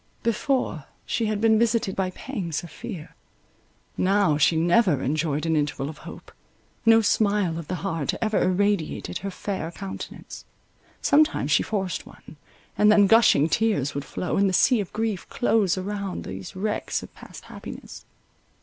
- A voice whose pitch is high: Yes, high, 195 Hz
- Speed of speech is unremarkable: Yes, average, 155 wpm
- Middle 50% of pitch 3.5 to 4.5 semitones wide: No, average, 4.9 semitones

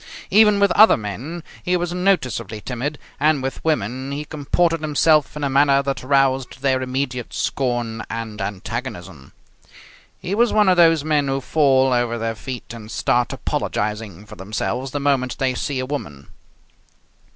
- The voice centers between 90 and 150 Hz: Yes, low, 135 Hz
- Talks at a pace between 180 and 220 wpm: No, average, 160 wpm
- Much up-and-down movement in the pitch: No, average, 4.4 semitones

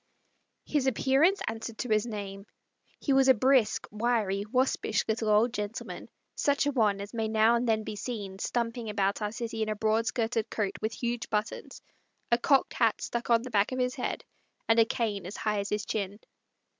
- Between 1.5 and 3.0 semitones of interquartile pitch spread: Yes, narrow, 2.4 semitones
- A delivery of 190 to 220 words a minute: Yes, average, 195 wpm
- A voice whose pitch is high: Yes, high, 225 Hz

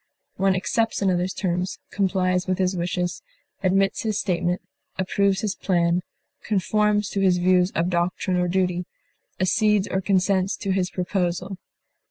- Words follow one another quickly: No, average, 140 wpm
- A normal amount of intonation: No, narrow, 1.6 semitones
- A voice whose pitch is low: No, medium, 185 Hz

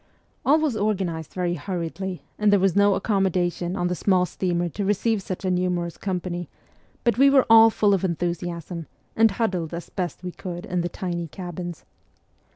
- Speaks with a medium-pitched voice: Yes, medium, 180 Hz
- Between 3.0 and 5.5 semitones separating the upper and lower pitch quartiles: No, narrow, 2.5 semitones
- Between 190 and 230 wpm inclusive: No, average, 175 wpm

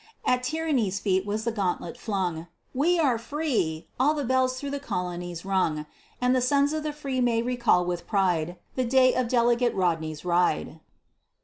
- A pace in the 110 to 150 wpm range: No, average, 175 wpm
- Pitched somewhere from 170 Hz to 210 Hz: No, high, 235 Hz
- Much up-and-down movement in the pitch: Yes, wide, 6.4 semitones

